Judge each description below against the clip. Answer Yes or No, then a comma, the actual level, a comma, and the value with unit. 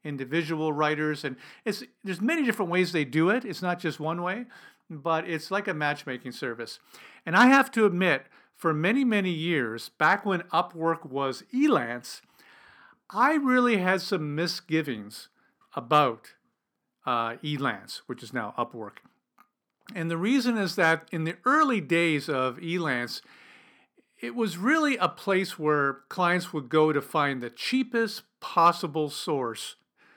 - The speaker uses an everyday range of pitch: Yes, average, 4.9 semitones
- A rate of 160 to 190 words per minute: No, average, 145 wpm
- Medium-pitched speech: Yes, medium, 170 Hz